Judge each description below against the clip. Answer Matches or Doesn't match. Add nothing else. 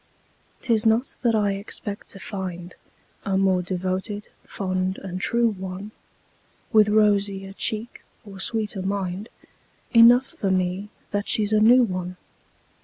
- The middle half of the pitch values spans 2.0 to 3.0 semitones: Matches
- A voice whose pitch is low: Doesn't match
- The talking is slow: Matches